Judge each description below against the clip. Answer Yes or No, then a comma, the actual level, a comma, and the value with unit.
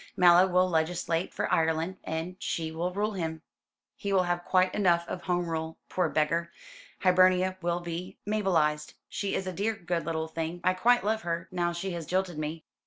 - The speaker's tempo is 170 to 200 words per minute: Yes, average, 185 wpm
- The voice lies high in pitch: No, medium, 175 Hz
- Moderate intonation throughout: No, narrow, 2.2 semitones